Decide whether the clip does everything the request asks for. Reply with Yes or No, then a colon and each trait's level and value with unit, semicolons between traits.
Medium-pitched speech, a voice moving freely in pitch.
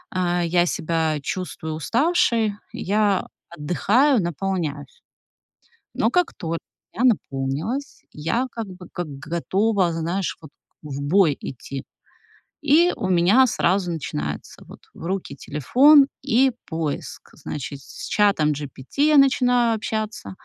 Yes: medium, 180 Hz; wide, 6.8 semitones